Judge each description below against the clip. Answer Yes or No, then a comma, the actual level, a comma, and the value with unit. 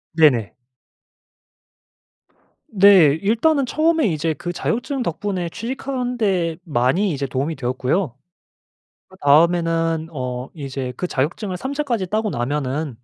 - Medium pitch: Yes, medium, 170 Hz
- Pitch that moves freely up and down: Yes, wide, 7.1 semitones